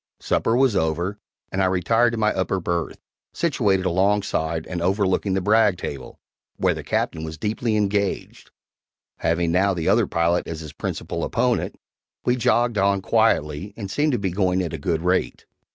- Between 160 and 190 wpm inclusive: Yes, average, 170 wpm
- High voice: No, very low, 95 Hz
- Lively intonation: No, average, 3.7 semitones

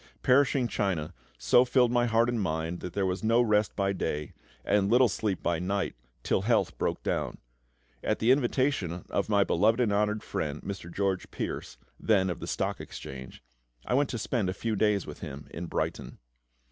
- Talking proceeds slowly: No, average, 185 wpm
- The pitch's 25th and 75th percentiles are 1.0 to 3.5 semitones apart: No, average, 4.5 semitones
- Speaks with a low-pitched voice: Yes, low, 100 Hz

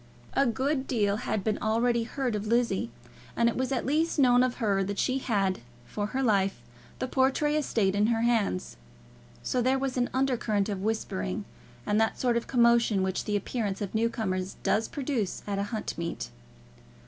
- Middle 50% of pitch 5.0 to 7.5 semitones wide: No, average, 4.0 semitones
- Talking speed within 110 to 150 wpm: No, average, 185 wpm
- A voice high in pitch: Yes, high, 225 Hz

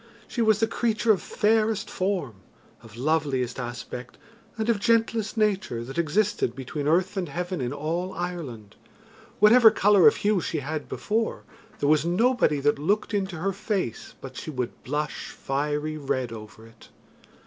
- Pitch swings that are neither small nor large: No, wide, 7.5 semitones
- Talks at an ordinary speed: Yes, average, 160 wpm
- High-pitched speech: No, medium, 170 Hz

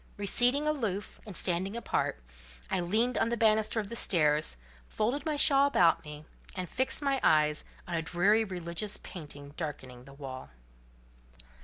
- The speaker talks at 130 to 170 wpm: Yes, average, 155 wpm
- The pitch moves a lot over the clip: Yes, wide, 7.1 semitones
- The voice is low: No, high, 190 Hz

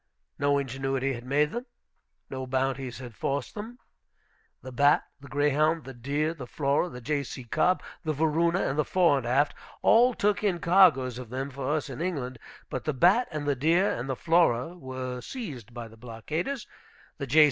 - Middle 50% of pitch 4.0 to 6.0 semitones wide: Yes, average, 4.3 semitones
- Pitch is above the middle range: No, medium, 140 Hz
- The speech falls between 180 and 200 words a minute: Yes, average, 185 wpm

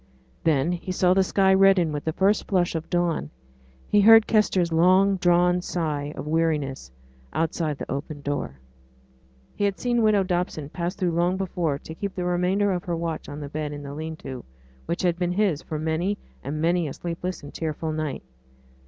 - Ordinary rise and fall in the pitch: Yes, average, 3.2 semitones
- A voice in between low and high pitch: Yes, medium, 170 Hz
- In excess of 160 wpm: Yes, average, 190 wpm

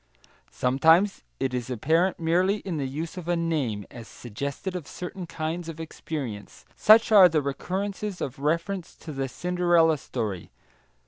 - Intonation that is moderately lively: Yes, average, 4.9 semitones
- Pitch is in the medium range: Yes, medium, 160 Hz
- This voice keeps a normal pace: Yes, average, 150 wpm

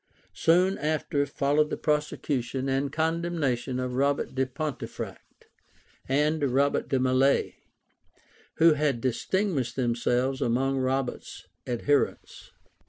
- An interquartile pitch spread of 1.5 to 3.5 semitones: Yes, average, 2.8 semitones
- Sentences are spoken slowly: Yes, slow, 100 wpm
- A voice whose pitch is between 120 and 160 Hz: Yes, low, 135 Hz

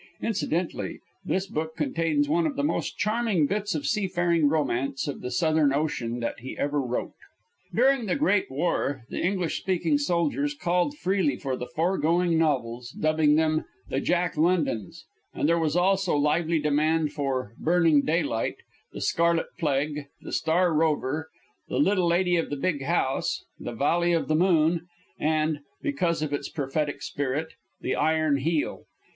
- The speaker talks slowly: No, average, 155 wpm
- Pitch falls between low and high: Yes, medium, 160 Hz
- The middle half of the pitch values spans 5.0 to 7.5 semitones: No, average, 3.5 semitones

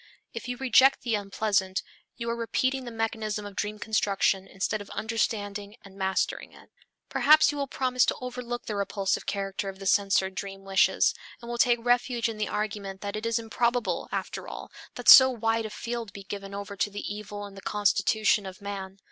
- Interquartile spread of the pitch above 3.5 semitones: No, average, 2.9 semitones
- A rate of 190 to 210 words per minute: Yes, average, 195 wpm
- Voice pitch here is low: No, high, 210 Hz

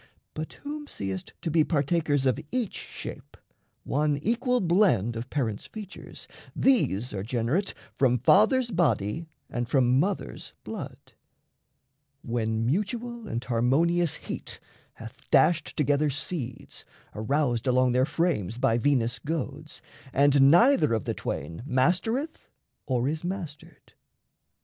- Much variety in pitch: Yes, wide, 6.6 semitones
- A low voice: No, medium, 145 Hz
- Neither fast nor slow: No, slow, 120 wpm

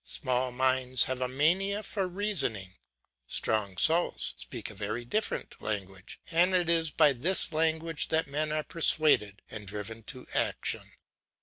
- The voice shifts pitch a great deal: Yes, wide, 6.8 semitones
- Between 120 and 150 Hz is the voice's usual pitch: Yes, medium, 140 Hz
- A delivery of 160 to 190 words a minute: No, average, 145 wpm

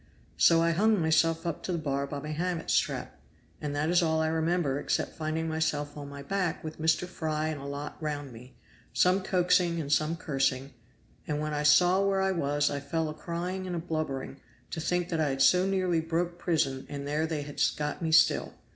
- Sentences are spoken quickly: Yes, fast, 210 wpm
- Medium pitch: Yes, medium, 160 Hz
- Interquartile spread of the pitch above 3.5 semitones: No, average, 2.9 semitones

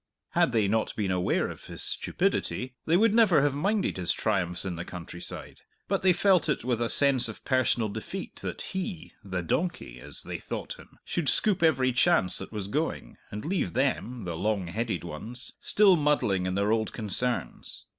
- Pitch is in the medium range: No, low, 120 Hz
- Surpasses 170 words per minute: Yes, average, 185 wpm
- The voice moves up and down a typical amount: No, wide, 8.4 semitones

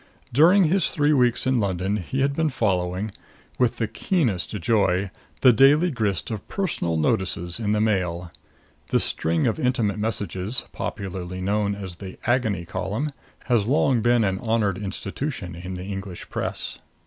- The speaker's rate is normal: Yes, average, 155 wpm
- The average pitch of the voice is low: Yes, low, 105 Hz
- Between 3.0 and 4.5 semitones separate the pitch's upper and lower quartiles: No, average, 5.0 semitones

